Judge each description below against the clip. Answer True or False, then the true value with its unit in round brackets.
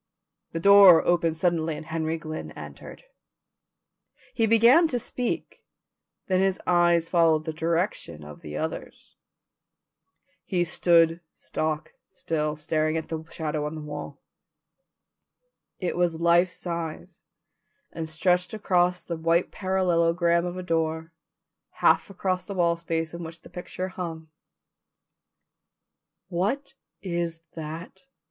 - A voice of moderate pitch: True (170 Hz)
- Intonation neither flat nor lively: False (2.1 semitones)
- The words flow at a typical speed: False (125 wpm)